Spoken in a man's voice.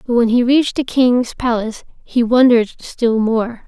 No: female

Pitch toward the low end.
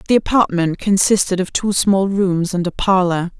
No: high, 190 Hz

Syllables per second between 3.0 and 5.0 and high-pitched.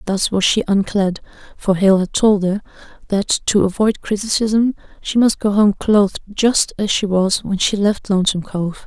Yes: 4.7 syllables/s; high, 200 Hz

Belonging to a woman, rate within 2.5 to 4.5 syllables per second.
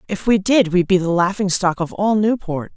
No: female; 5.1 syllables/s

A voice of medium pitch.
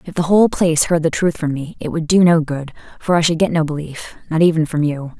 Yes: medium, 160 Hz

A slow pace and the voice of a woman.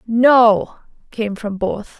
Yes: slow, 120 wpm; female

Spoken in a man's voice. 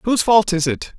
Yes: male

